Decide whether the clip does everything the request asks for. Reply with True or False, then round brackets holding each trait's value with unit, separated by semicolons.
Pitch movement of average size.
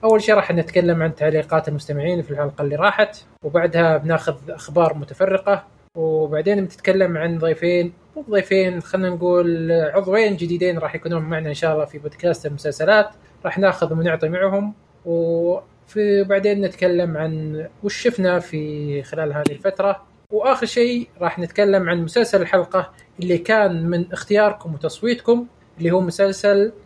True (3.7 semitones)